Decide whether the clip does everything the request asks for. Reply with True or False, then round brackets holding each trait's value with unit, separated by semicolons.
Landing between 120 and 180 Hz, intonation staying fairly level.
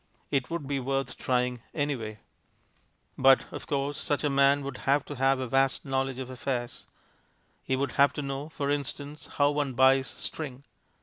True (135 Hz; 1.5 semitones)